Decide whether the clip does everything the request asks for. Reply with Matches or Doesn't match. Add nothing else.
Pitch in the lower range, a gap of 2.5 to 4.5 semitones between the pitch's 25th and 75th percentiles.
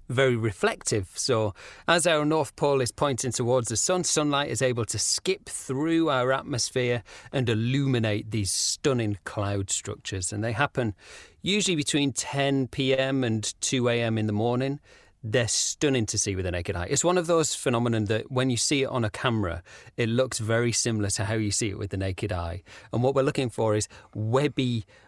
Matches